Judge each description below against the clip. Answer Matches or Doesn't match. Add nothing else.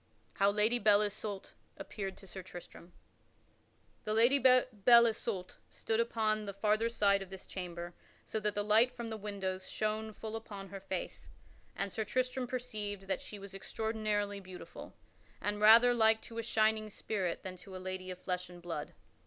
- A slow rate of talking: Doesn't match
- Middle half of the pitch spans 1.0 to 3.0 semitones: Matches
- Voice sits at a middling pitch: Doesn't match